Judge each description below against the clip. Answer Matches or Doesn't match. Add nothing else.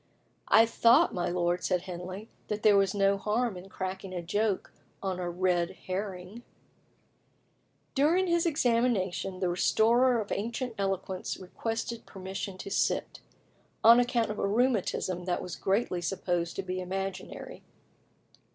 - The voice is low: Doesn't match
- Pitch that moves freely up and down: Doesn't match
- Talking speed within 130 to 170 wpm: Matches